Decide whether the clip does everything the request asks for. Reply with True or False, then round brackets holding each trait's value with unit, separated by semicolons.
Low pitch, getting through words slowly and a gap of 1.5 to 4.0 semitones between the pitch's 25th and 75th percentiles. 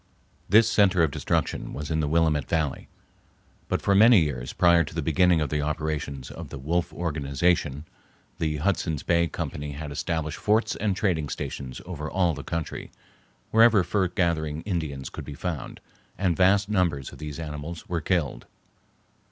False (80 Hz; 165 wpm; 3.5 semitones)